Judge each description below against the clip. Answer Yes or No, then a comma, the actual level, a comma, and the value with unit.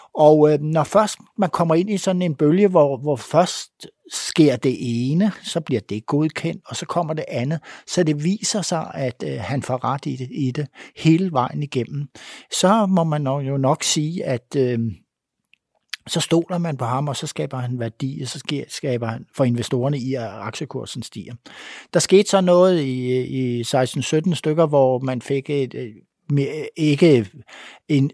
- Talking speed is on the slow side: No, average, 190 wpm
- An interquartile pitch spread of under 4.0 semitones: No, average, 4.5 semitones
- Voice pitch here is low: No, medium, 145 Hz